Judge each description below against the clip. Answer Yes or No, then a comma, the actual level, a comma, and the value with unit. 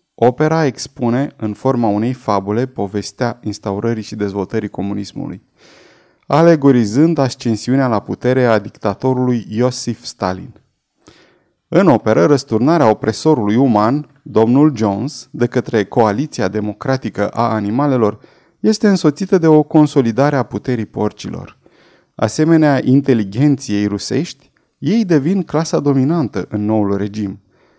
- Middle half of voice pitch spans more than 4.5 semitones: Yes, average, 5.2 semitones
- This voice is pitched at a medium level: No, low, 120 Hz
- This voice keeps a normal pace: No, slow, 110 wpm